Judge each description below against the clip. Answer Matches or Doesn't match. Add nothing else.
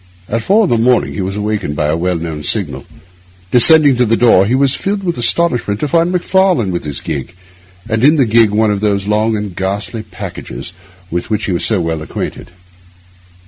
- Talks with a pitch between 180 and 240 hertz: Doesn't match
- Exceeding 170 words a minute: Matches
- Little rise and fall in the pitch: Doesn't match